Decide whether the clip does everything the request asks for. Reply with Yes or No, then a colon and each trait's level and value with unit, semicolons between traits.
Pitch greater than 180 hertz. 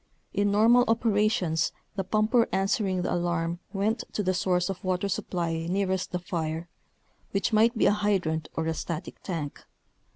Yes: high, 190 Hz